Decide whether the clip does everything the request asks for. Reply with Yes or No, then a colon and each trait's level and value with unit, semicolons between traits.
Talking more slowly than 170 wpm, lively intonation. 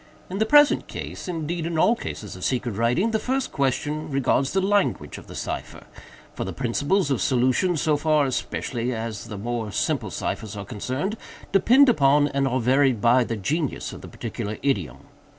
No: average, 175 wpm; wide, 6.4 semitones